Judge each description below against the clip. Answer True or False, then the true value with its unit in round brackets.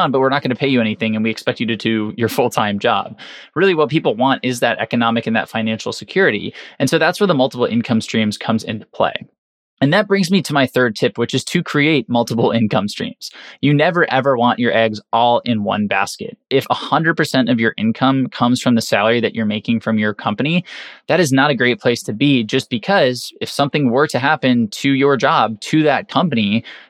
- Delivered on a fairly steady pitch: False (3.8 semitones)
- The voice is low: True (125 Hz)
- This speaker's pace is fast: True (225 wpm)